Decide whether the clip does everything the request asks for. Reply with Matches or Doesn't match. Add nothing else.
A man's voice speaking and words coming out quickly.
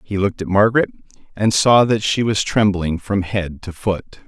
Doesn't match